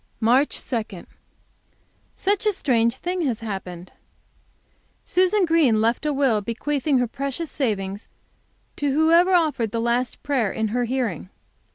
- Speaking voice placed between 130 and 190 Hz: No, very high, 250 Hz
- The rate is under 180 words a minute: Yes, slow, 135 wpm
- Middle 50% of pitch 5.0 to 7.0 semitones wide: Yes, wide, 5.4 semitones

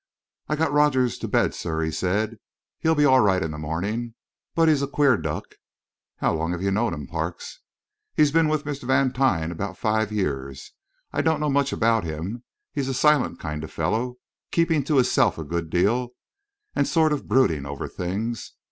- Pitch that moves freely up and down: Yes, wide, 8.6 semitones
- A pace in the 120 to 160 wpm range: No, average, 190 wpm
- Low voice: Yes, low, 115 Hz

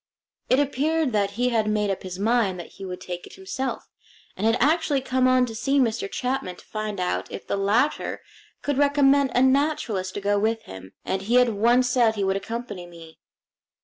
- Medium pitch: No, high, 230 Hz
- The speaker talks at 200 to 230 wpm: Yes, fast, 205 wpm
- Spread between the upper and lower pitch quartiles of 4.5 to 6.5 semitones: Yes, average, 4.9 semitones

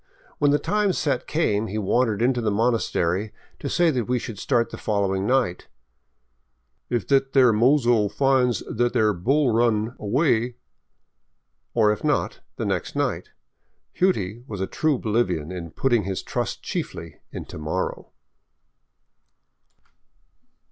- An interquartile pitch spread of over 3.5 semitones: Yes, average, 4.6 semitones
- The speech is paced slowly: No, average, 160 wpm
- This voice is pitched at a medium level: No, low, 115 Hz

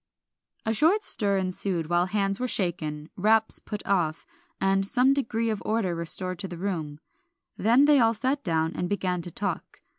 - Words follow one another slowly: No, average, 175 wpm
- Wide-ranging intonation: No, average, 4.3 semitones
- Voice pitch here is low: No, high, 195 Hz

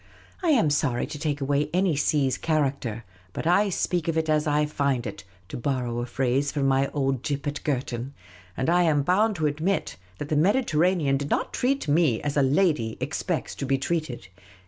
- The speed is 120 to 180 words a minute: No, average, 195 wpm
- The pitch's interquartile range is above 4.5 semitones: No, average, 3.3 semitones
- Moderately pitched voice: Yes, medium, 145 Hz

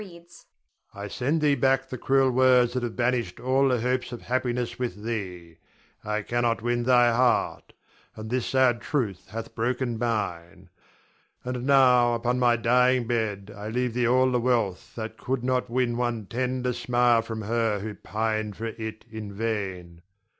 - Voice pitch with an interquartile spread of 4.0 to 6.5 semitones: No, narrow, 2.5 semitones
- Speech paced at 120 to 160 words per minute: No, average, 170 wpm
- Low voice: Yes, low, 120 Hz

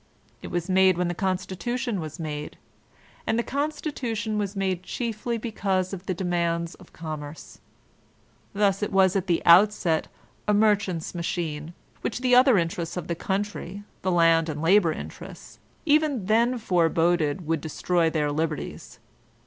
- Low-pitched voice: No, medium, 185 Hz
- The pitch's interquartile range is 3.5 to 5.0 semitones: Yes, average, 4.0 semitones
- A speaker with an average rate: Yes, average, 150 wpm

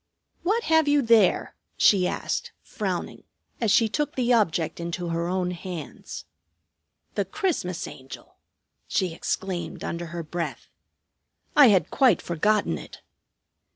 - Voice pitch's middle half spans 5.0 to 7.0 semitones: Yes, wide, 5.5 semitones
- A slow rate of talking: Yes, slow, 125 wpm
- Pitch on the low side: No, medium, 185 Hz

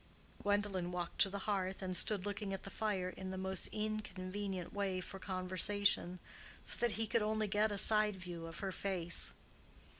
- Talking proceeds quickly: No, average, 180 wpm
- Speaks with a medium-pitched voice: No, high, 195 Hz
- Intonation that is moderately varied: No, narrow, 2.0 semitones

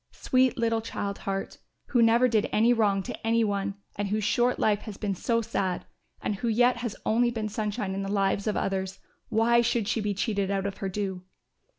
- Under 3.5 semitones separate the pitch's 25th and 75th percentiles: Yes, average, 2.7 semitones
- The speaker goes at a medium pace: No, fast, 210 wpm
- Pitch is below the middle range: No, high, 210 Hz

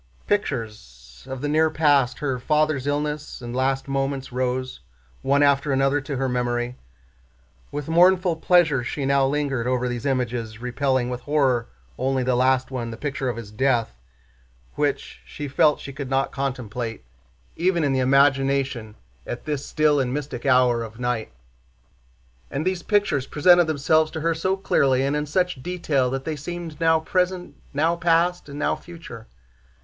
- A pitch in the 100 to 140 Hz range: Yes, low, 135 Hz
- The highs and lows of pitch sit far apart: No, average, 3.4 semitones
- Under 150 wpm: No, average, 155 wpm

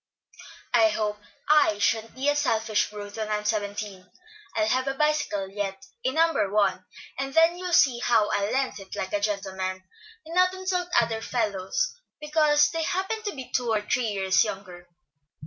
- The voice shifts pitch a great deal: Yes, wide, 6.4 semitones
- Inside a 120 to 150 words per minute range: No, average, 175 wpm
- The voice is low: No, high, 225 Hz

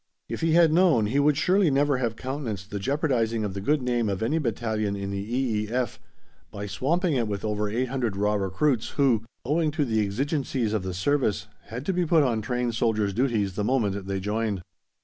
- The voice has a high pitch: No, low, 115 Hz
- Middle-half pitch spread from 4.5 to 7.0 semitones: Yes, average, 5.2 semitones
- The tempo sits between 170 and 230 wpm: Yes, average, 200 wpm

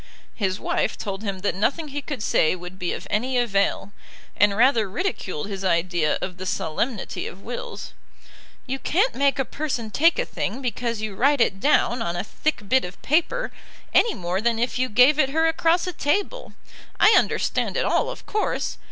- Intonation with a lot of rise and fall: Yes, wide, 7.2 semitones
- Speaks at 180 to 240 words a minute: Yes, average, 190 wpm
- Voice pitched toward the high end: Yes, high, 235 Hz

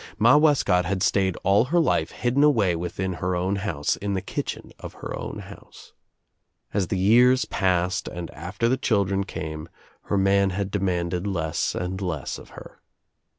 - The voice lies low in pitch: Yes, very low, 95 Hz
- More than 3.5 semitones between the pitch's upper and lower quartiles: No, narrow, 2.5 semitones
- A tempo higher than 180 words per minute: No, average, 165 wpm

